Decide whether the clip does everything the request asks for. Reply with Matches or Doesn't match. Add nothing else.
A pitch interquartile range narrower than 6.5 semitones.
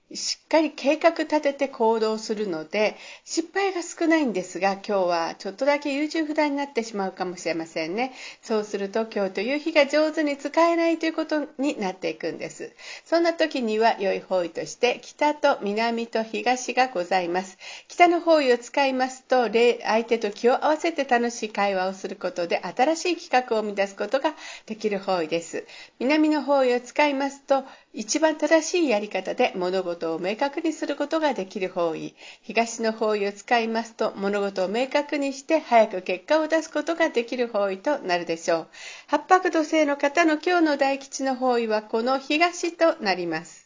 Doesn't match